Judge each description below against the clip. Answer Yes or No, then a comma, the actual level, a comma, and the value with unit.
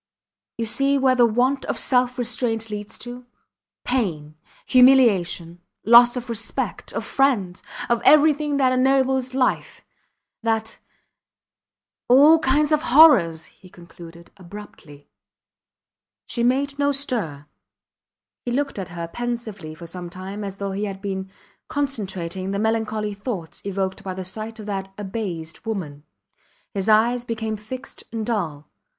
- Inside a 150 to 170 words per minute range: No, slow, 135 wpm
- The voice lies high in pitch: Yes, high, 220 Hz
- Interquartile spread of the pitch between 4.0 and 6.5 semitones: Yes, average, 5.2 semitones